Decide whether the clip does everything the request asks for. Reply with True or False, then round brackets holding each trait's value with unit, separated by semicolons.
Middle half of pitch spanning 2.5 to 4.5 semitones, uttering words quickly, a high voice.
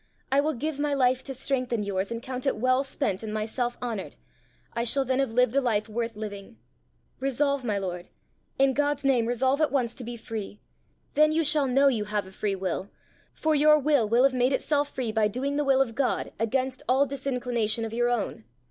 True (3.6 semitones; 210 wpm; 250 Hz)